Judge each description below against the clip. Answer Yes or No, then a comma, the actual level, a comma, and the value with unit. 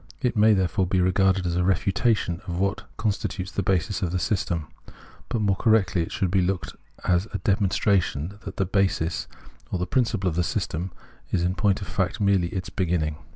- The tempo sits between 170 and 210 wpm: Yes, average, 200 wpm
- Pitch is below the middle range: Yes, very low, 95 Hz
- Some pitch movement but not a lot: No, narrow, 2.1 semitones